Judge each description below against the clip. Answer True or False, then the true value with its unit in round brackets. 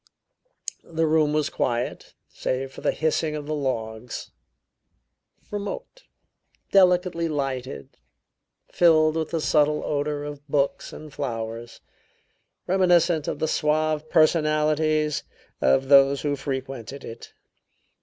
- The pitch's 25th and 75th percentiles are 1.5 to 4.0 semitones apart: True (2.7 semitones)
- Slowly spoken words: True (110 wpm)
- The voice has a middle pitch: True (150 Hz)